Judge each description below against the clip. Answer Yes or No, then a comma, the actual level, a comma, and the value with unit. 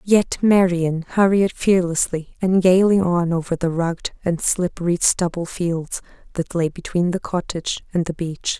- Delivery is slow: No, average, 155 wpm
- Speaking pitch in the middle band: Yes, medium, 175 Hz